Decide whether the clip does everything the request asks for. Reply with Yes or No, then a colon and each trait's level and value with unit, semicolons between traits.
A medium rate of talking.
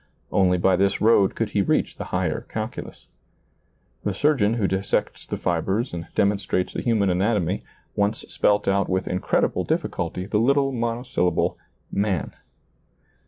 Yes: average, 150 wpm